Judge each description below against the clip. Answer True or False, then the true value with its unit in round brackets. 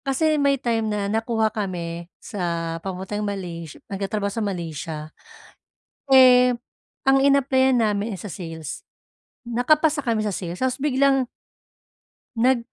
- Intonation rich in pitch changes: True (6.1 semitones)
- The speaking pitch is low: False (215 Hz)